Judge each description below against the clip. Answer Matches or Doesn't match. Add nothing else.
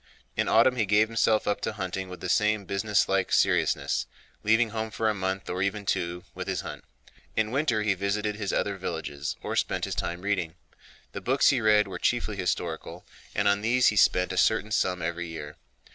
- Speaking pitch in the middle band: Doesn't match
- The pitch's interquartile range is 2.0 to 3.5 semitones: Matches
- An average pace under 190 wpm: Doesn't match